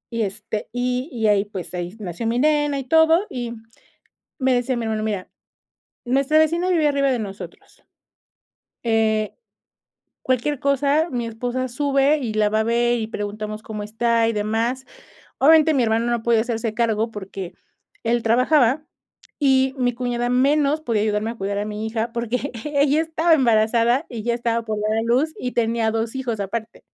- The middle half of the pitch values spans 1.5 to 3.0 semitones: No, average, 3.5 semitones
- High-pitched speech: Yes, high, 235 Hz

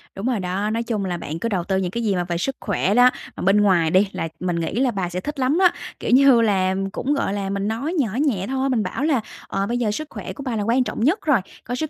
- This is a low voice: No, high, 215 Hz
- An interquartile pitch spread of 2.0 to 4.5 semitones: No, average, 5.3 semitones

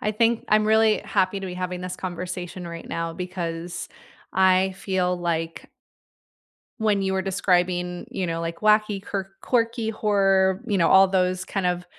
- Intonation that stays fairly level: Yes, narrow, 2.2 semitones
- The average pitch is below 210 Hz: Yes, high, 190 Hz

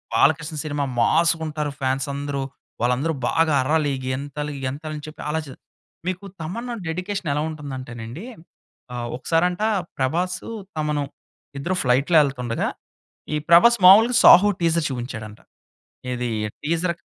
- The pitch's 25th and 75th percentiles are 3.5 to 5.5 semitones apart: Yes, average, 4.0 semitones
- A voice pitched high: No, medium, 150 Hz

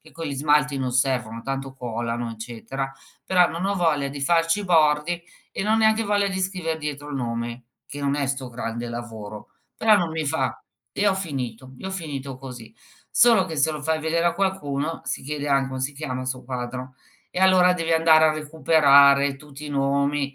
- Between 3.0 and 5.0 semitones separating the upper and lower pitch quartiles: Yes, average, 4.0 semitones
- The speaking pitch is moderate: Yes, medium, 145 Hz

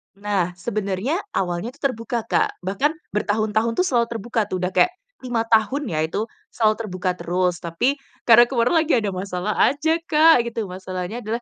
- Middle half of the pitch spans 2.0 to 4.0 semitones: No, average, 4.7 semitones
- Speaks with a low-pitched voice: No, high, 215 Hz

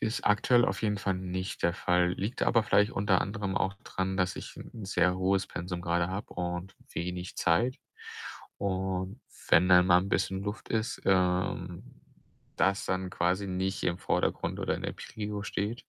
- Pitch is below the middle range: Yes, very low, 95 Hz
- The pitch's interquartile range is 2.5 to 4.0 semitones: No, narrow, 2.1 semitones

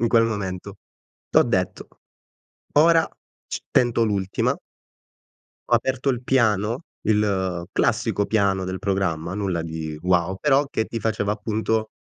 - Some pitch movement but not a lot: Yes, average, 3.4 semitones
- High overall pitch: No, low, 105 Hz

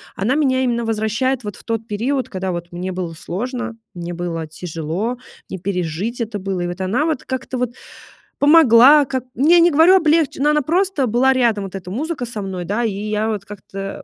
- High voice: Yes, high, 225 Hz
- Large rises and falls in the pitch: Yes, wide, 5.7 semitones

